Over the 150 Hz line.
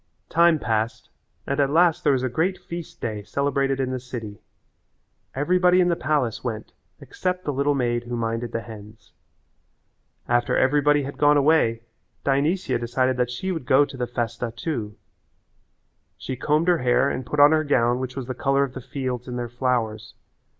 No: low, 130 Hz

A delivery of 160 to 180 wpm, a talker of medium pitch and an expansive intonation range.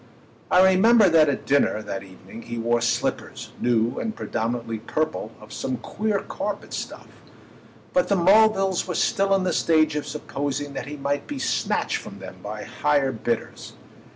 Yes: average, 165 wpm; medium, 145 Hz; wide, 8.1 semitones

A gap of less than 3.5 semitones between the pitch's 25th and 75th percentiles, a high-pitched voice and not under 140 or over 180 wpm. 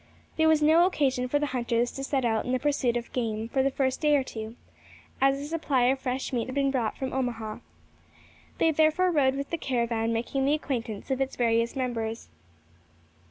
No: average, 3.1 semitones; very high, 260 Hz; fast, 205 wpm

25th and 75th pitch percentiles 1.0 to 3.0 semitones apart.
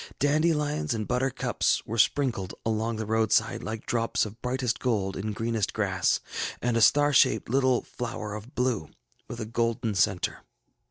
Yes: average, 2.7 semitones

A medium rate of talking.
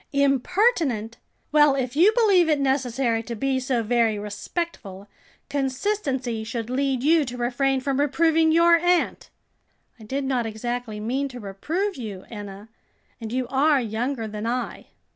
Yes: average, 145 wpm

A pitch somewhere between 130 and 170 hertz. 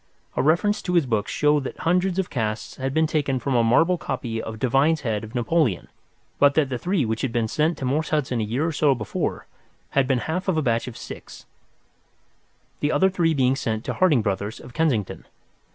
Yes: low, 135 Hz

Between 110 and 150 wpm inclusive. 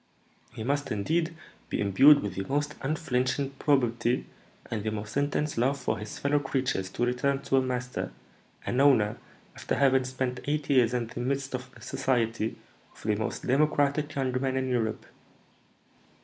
No: average, 165 wpm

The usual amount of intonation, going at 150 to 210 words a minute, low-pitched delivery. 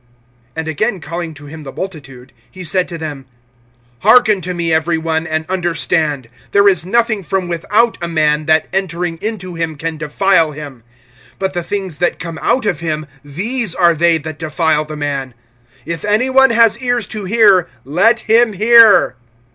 No: average, 4.3 semitones; average, 175 wpm; medium, 170 Hz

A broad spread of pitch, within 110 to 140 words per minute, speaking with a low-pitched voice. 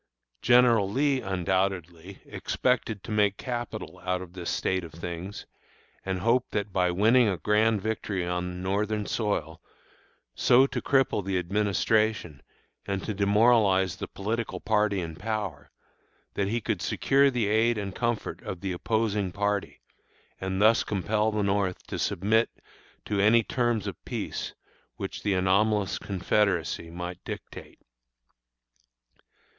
No: average, 3.0 semitones; slow, 135 wpm; low, 100 Hz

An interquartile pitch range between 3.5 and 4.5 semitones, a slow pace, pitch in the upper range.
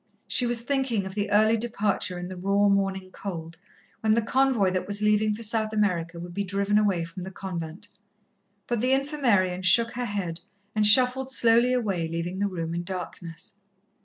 No: average, 4.0 semitones; average, 185 wpm; high, 200 Hz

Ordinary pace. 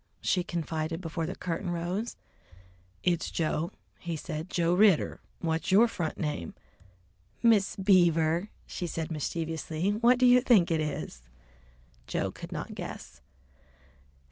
No: slow, 130 wpm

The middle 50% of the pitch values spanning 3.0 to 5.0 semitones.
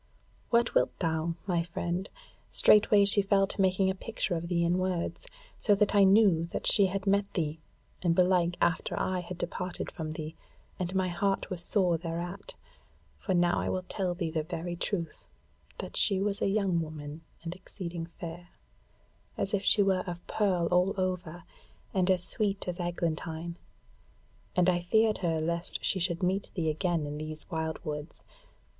No: narrow, 2.5 semitones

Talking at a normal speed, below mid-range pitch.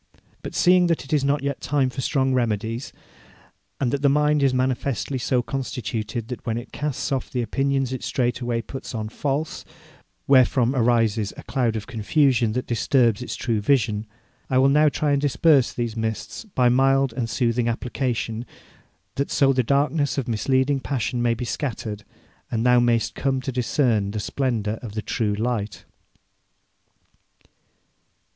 Yes: average, 165 wpm; low, 125 Hz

